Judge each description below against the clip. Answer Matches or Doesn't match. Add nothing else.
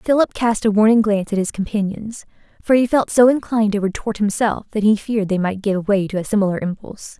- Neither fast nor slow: Doesn't match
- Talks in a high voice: Matches